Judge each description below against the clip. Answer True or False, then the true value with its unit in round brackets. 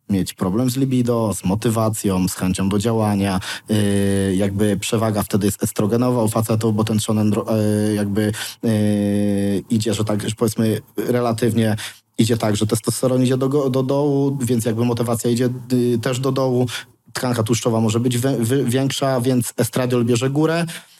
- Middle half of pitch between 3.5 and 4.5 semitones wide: False (2.9 semitones)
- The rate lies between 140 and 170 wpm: True (155 wpm)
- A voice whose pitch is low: True (115 Hz)